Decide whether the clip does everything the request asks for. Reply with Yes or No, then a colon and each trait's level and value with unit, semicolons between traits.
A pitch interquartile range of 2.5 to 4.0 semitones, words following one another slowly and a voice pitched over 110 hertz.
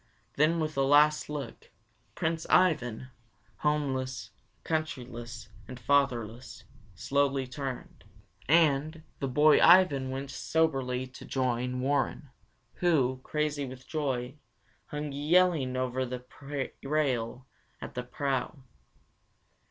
Yes: average, 3.0 semitones; slow, 105 wpm; low, 135 Hz